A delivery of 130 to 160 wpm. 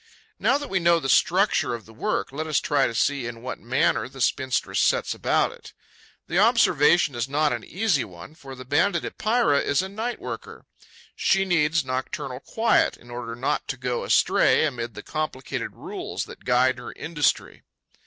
No: average, 185 wpm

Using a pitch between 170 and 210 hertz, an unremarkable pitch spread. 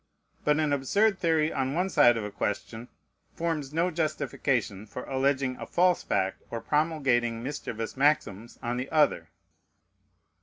No: low, 135 Hz; average, 4.8 semitones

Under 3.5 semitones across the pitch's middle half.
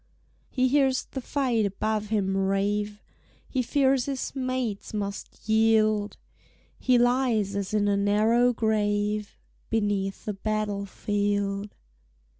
Yes: average, 3.1 semitones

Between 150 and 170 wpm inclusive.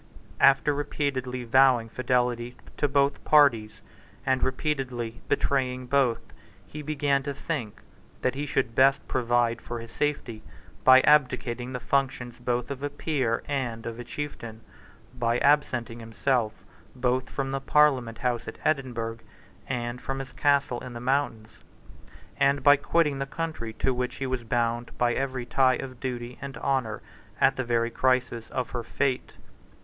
Yes: average, 155 wpm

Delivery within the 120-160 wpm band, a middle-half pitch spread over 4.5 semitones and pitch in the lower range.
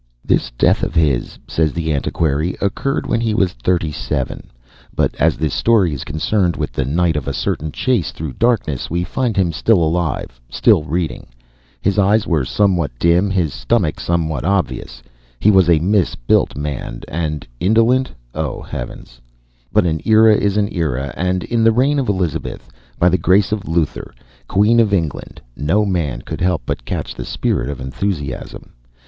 No: average, 175 wpm; average, 5.1 semitones; very low, 85 Hz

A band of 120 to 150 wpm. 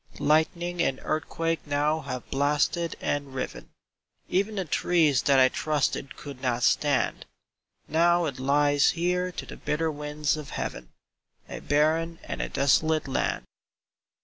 Yes: average, 140 wpm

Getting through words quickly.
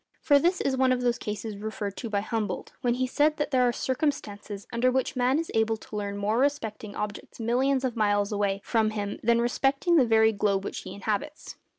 Yes: fast, 215 wpm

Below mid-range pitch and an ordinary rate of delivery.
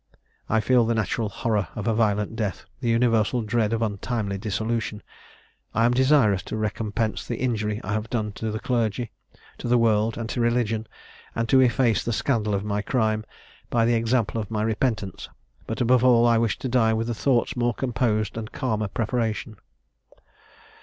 Yes: low, 115 Hz; average, 180 wpm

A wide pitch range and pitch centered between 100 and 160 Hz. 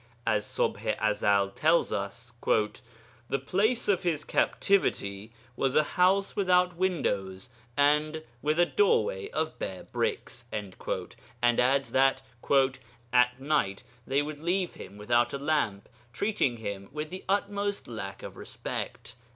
Yes: wide, 7.8 semitones; low, 135 Hz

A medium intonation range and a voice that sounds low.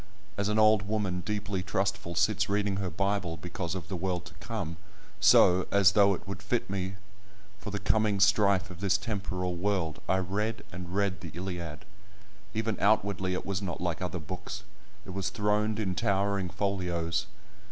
No: narrow, 2.2 semitones; very low, 95 Hz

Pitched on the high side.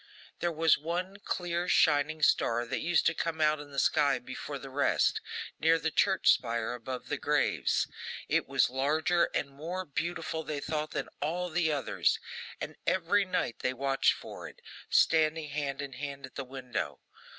No: medium, 150 Hz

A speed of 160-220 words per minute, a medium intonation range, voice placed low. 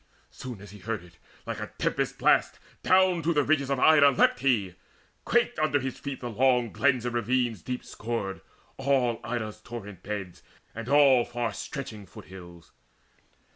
Yes: average, 170 wpm; average, 4.8 semitones; low, 120 Hz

